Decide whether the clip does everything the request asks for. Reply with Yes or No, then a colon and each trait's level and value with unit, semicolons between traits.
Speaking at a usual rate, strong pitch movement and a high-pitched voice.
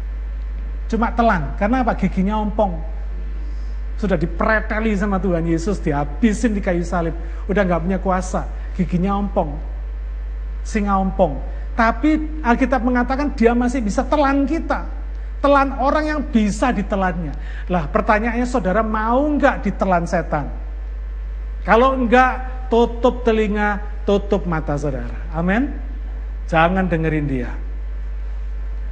Yes: average, 110 wpm; wide, 8.2 semitones; high, 195 Hz